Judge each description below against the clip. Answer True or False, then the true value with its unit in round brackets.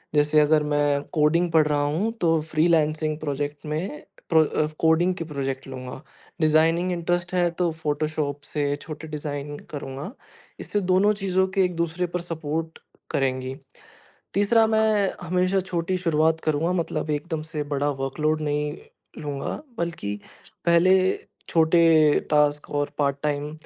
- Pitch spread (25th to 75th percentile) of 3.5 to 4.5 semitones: False (2.7 semitones)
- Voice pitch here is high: False (155 Hz)